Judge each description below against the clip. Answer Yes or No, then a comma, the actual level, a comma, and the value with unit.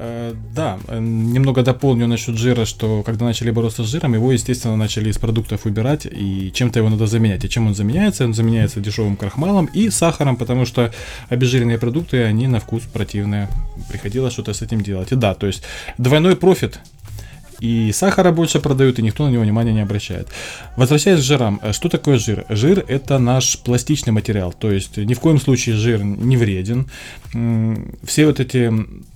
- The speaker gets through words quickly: Yes, fast, 175 wpm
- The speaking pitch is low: Yes, low, 115 Hz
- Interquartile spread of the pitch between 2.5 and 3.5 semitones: Yes, average, 3.2 semitones